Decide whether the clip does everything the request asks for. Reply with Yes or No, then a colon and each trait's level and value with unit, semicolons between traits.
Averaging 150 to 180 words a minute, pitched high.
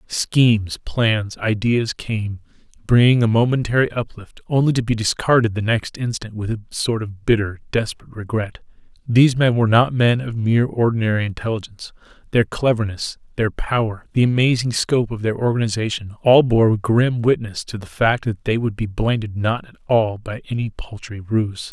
No: average, 165 wpm; low, 115 Hz